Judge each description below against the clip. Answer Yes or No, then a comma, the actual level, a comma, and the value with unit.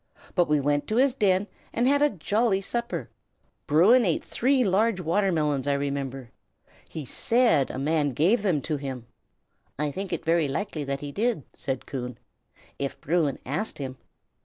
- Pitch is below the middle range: No, medium, 160 Hz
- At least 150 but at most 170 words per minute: Yes, average, 165 wpm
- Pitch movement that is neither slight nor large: No, wide, 6.9 semitones